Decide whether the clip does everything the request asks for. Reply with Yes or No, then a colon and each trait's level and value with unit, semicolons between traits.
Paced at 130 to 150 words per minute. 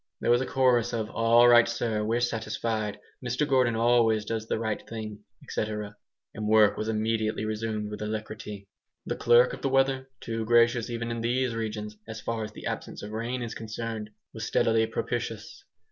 No: average, 180 wpm